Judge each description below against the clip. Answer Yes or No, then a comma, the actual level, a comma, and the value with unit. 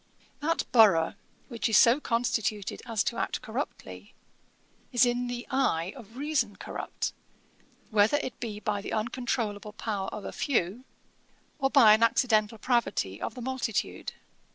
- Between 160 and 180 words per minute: No, average, 145 wpm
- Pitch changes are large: No, average, 3.1 semitones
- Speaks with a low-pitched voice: No, high, 230 Hz